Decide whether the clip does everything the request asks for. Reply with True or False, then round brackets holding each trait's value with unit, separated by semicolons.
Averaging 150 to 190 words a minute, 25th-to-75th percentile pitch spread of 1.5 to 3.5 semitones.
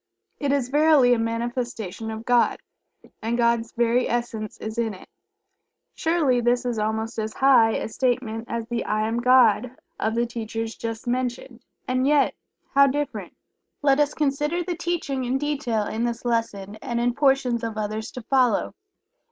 True (165 wpm; 2.8 semitones)